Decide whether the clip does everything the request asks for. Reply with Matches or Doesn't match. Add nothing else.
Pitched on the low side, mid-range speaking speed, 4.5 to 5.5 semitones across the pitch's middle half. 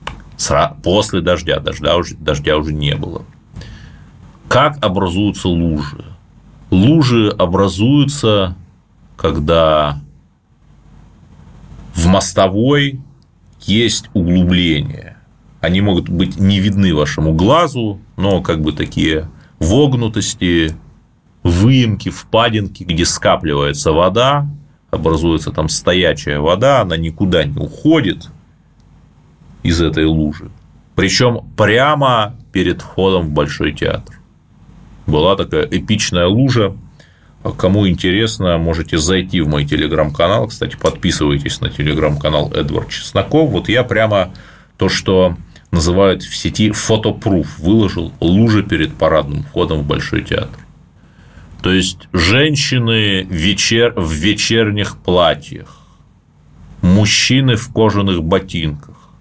Doesn't match